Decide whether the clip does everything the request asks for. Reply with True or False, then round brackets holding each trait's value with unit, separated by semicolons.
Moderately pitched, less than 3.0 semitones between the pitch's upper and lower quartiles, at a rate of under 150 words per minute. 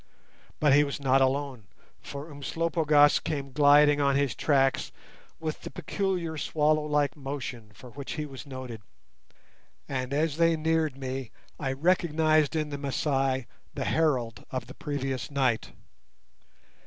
True (145 Hz; 2.5 semitones; 140 wpm)